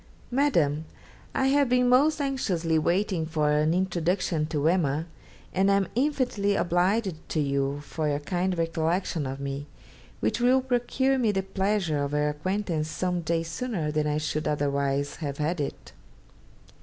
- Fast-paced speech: No, average, 155 wpm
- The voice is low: No, medium, 170 Hz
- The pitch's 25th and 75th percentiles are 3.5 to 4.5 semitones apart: No, average, 5.2 semitones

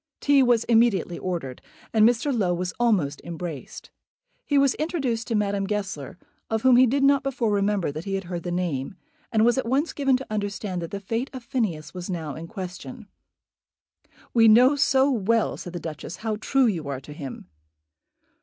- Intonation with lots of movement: Yes, wide, 5.8 semitones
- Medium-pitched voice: No, high, 210 Hz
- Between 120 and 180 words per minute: No, average, 190 wpm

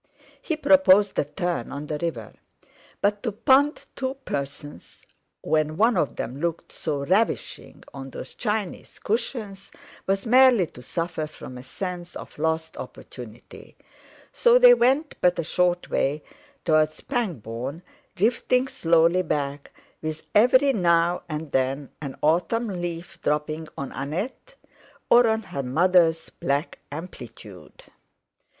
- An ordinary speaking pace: No, slow, 130 wpm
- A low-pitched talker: No, medium, 170 Hz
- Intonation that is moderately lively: No, wide, 6.7 semitones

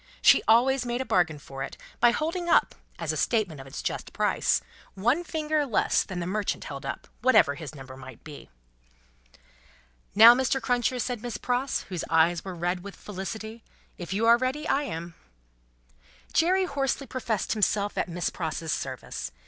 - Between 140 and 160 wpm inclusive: No, average, 175 wpm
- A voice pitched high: Yes, high, 215 Hz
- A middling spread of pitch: No, wide, 7.1 semitones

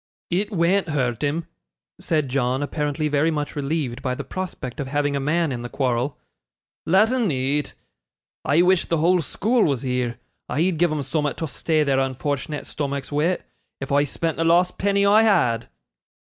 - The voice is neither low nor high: Yes, medium, 150 Hz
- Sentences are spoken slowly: No, average, 175 wpm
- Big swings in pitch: No, average, 3.9 semitones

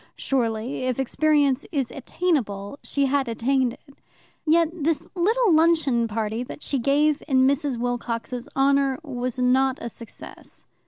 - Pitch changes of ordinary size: Yes, average, 3.3 semitones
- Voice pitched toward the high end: Yes, very high, 270 Hz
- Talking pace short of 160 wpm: Yes, average, 140 wpm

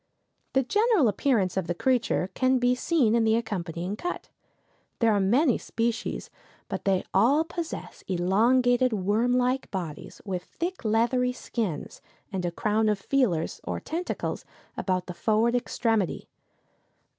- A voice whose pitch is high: Yes, high, 225 Hz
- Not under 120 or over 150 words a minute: Yes, average, 140 wpm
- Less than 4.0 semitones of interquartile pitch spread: No, average, 4.9 semitones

